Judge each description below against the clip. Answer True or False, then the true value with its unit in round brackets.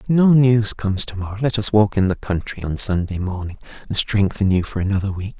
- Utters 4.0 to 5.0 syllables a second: False (5.8 syllables/s)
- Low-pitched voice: True (100 Hz)